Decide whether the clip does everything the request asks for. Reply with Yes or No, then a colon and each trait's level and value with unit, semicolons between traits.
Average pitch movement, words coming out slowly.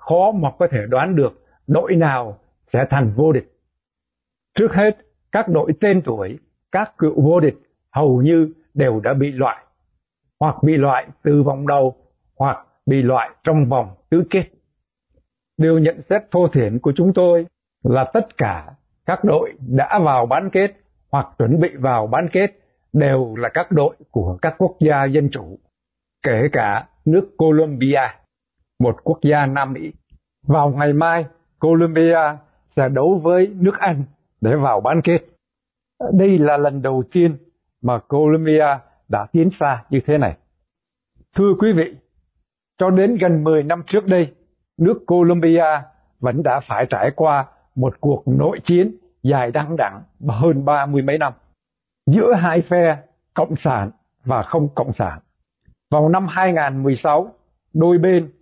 Yes: average, 4.3 semitones; slow, 155 wpm